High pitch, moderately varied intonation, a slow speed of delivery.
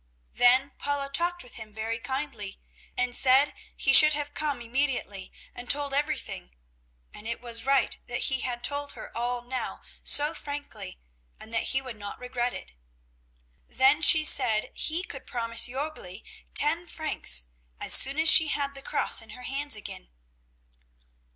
No: very high, 265 Hz; average, 3.8 semitones; average, 160 wpm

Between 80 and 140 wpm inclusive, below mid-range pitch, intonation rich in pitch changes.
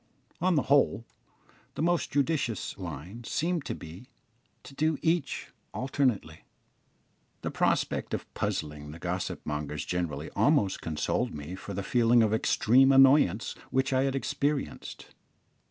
Yes: slow, 135 wpm; low, 115 Hz; wide, 7.8 semitones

